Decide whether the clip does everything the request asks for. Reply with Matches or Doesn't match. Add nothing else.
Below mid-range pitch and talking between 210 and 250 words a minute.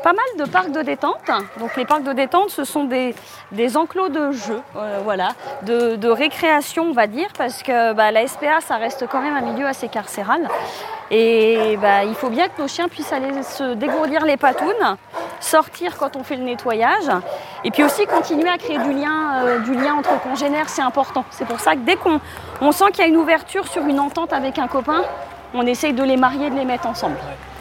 Doesn't match